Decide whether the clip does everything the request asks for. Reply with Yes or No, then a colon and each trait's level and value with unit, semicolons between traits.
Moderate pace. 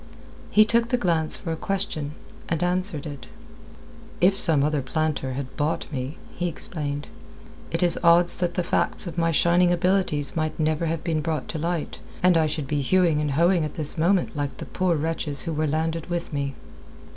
Yes: average, 190 wpm